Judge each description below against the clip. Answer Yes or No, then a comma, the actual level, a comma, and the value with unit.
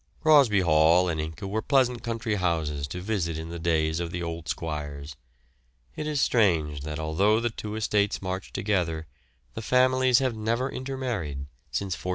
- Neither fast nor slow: Yes, average, 175 wpm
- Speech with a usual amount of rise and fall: No, wide, 6.4 semitones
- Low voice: Yes, very low, 95 Hz